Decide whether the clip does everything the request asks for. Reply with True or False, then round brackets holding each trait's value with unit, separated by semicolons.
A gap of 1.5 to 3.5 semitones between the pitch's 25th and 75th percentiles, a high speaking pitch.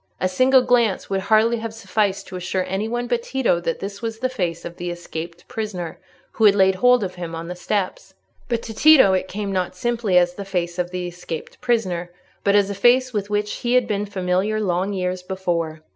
False (3.9 semitones; 195 Hz)